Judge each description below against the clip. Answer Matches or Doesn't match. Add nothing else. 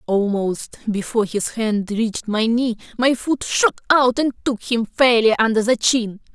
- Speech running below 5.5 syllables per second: Matches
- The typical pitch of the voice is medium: Doesn't match